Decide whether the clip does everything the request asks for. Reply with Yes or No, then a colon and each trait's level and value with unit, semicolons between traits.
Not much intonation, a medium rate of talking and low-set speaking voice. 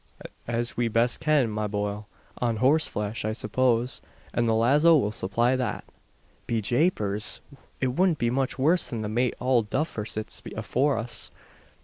No: average, 3.3 semitones; average, 155 wpm; low, 120 Hz